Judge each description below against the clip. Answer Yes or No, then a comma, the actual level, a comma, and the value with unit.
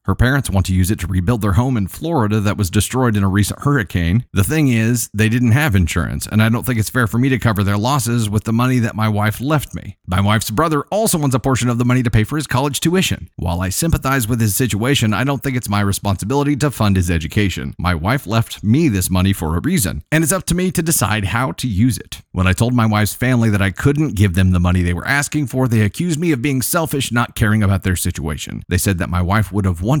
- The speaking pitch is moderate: No, low, 110 Hz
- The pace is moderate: No, fast, 270 wpm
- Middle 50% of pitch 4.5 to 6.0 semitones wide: Yes, average, 5.2 semitones